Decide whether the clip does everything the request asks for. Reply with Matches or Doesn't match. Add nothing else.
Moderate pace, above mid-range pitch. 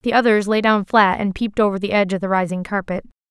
Doesn't match